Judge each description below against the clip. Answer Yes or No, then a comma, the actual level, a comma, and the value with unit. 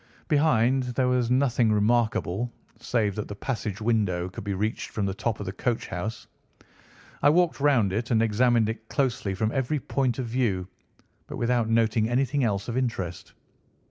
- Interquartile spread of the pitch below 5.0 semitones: Yes, average, 3.3 semitones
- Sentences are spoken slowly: No, average, 175 wpm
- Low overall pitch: Yes, low, 115 Hz